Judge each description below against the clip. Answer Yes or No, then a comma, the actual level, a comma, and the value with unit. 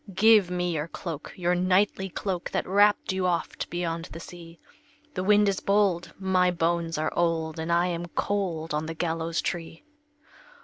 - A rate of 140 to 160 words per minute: No, average, 170 wpm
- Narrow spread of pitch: Yes, narrow, 2.3 semitones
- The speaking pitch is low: No, medium, 175 Hz